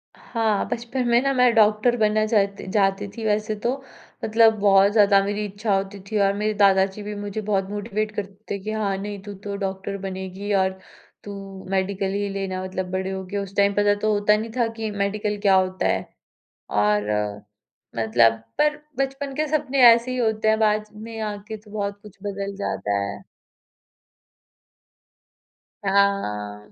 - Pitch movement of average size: No, narrow, 1.9 semitones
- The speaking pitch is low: No, high, 205 Hz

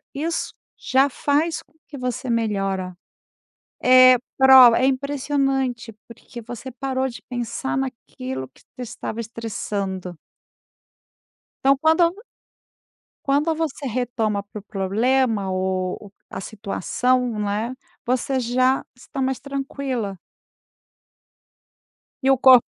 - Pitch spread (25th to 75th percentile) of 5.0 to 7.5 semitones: No, average, 4.0 semitones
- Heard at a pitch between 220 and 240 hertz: No, very high, 250 Hz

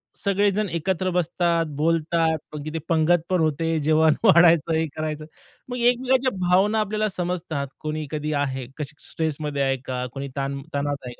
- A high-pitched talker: No, medium, 160 Hz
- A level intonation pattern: No, average, 3.2 semitones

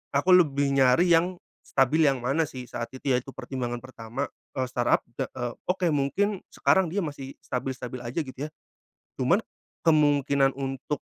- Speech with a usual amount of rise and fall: Yes, average, 3.6 semitones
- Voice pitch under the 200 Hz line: Yes, low, 135 Hz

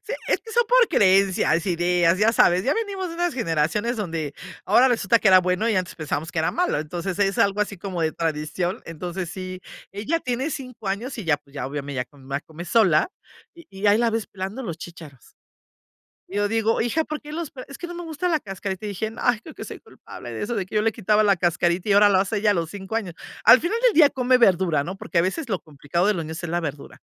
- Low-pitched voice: No, high, 195 Hz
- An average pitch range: No, wide, 5.7 semitones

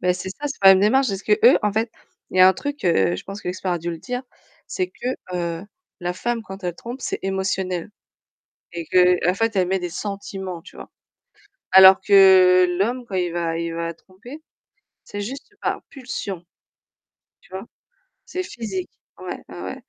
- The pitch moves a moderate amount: Yes, average, 3.6 semitones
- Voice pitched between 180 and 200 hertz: Yes, high, 190 Hz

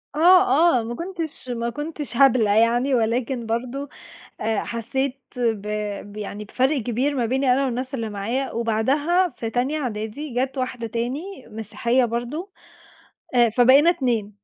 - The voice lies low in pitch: No, very high, 250 Hz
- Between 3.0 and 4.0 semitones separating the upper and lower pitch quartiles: Yes, average, 3.3 semitones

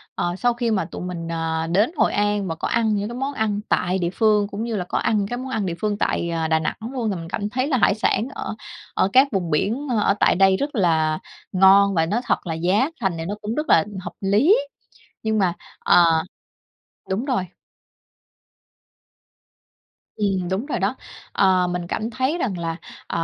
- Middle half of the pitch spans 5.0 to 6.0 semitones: No, average, 4.4 semitones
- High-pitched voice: Yes, high, 200 Hz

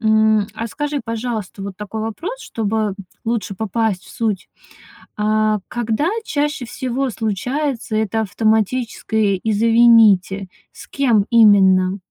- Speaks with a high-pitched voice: Yes, high, 220 Hz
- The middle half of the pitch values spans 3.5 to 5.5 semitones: No, narrow, 2.4 semitones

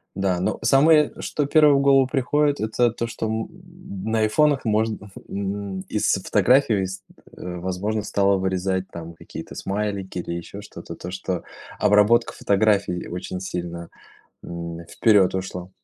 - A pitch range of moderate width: Yes, average, 3.7 semitones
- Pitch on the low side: Yes, low, 100 Hz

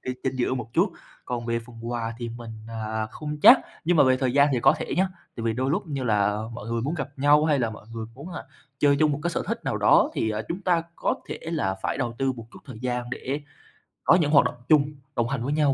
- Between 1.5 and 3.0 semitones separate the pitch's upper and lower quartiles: No, average, 4.1 semitones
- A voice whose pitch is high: No, low, 130 Hz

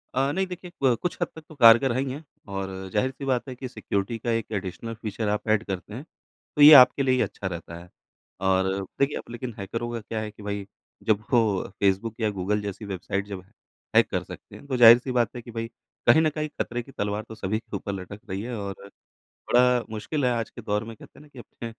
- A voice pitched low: Yes, low, 115 Hz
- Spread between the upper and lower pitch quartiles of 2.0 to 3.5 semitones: No, average, 3.9 semitones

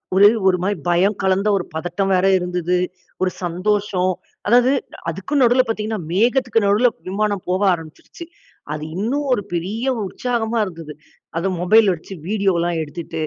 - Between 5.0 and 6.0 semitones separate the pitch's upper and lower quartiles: No, average, 3.8 semitones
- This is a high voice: Yes, high, 195 Hz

